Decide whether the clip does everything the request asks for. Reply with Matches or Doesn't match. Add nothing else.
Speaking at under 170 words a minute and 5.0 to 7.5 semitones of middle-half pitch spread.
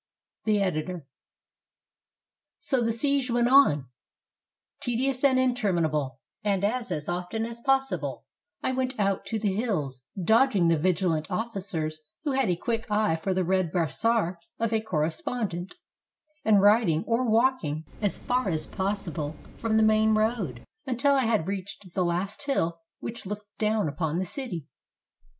Matches